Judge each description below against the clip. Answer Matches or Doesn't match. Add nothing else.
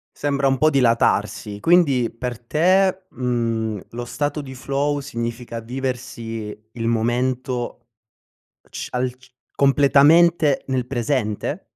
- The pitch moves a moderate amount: Matches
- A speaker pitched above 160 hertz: Doesn't match